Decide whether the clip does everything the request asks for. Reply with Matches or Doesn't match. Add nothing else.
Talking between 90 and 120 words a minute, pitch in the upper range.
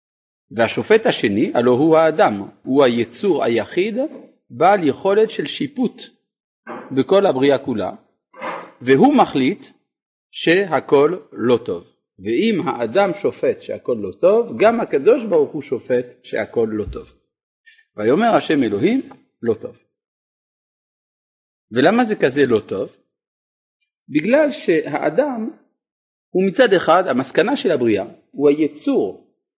Matches